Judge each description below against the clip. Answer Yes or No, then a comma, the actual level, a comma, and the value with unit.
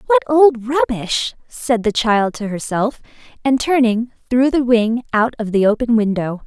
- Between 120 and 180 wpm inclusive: Yes, average, 165 wpm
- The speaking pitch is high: Yes, high, 235 Hz